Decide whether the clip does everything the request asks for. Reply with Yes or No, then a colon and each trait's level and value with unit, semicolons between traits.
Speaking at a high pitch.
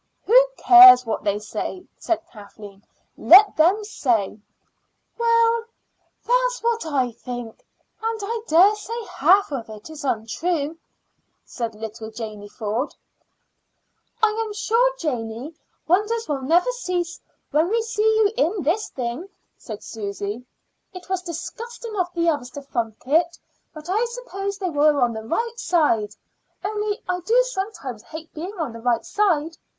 Yes: very high, 330 Hz